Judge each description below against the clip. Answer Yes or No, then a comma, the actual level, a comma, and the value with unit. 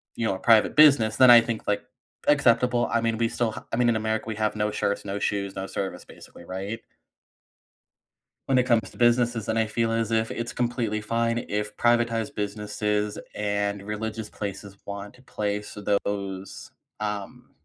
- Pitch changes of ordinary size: No, narrow, 2.2 semitones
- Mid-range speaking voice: No, low, 110 Hz